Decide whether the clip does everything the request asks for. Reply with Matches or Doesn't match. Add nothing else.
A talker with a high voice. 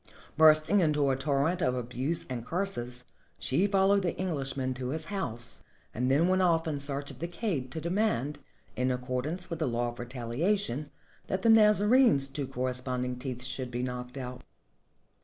Doesn't match